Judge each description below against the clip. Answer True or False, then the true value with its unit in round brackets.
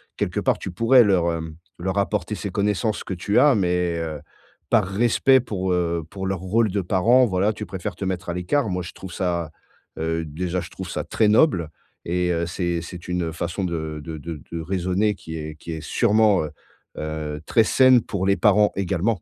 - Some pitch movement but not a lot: True (3.5 semitones)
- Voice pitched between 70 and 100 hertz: True (90 Hz)